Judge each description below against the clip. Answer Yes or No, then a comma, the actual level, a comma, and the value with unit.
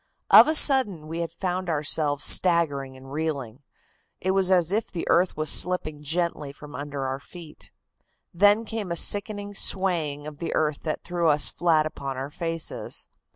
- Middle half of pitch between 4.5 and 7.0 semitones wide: No, average, 3.8 semitones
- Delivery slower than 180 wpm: Yes, average, 170 wpm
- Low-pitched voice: No, medium, 165 Hz